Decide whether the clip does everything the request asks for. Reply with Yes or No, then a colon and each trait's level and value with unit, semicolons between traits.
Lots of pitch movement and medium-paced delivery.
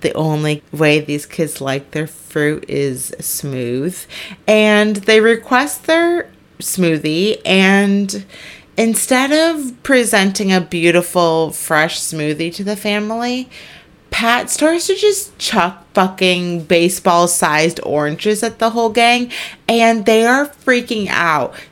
No: wide, 6.2 semitones; slow, 120 wpm